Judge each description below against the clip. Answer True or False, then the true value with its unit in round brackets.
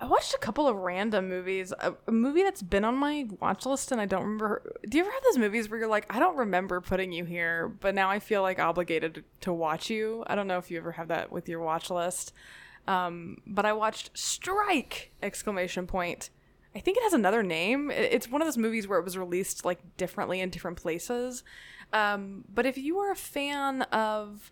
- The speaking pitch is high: True (205 Hz)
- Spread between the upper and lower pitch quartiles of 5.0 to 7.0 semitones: True (5.4 semitones)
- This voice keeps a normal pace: False (220 wpm)